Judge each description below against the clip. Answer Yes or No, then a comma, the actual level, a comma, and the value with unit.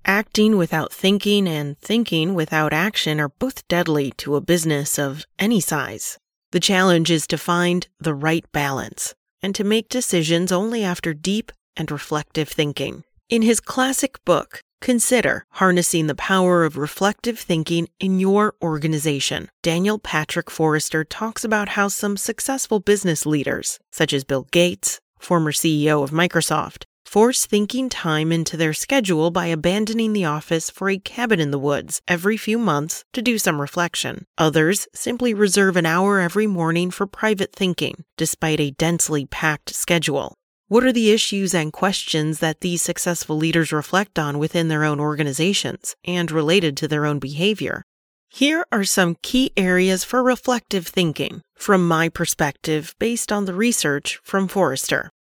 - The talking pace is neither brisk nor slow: Yes, average, 155 wpm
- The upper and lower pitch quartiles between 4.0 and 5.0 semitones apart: Yes, average, 4.7 semitones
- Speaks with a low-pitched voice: No, medium, 175 Hz